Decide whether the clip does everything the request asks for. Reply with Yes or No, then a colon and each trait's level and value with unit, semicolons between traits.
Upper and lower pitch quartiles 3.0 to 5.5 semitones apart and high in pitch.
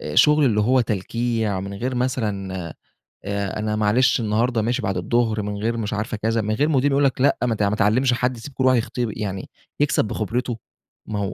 No: average, 3.3 semitones; low, 115 Hz